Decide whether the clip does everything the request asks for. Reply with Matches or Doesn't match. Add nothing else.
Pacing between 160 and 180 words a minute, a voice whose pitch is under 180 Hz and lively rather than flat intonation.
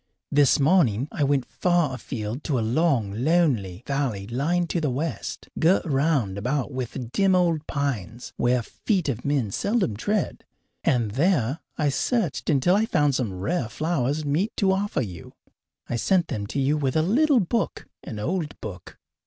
Matches